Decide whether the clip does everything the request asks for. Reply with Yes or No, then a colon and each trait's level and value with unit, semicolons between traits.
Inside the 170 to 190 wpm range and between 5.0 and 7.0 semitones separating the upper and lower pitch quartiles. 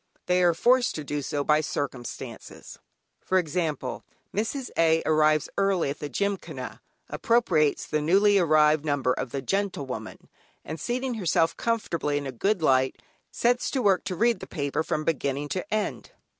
No: average, 160 wpm; wide, 5.5 semitones